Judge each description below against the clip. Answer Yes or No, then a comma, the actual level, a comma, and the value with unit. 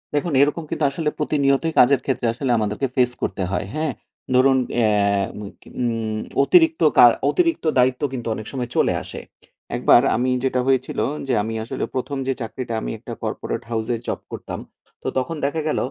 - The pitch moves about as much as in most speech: Yes, average, 3.3 semitones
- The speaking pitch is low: Yes, low, 130 Hz